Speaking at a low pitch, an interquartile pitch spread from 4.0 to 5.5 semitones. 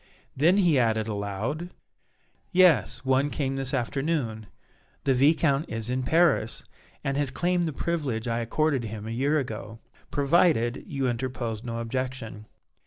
Yes: low, 130 Hz; average, 4.5 semitones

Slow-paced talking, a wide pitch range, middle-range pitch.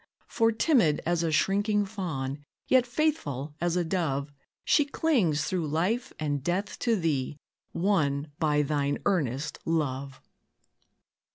Yes: slow, 125 wpm; wide, 5.9 semitones; medium, 165 Hz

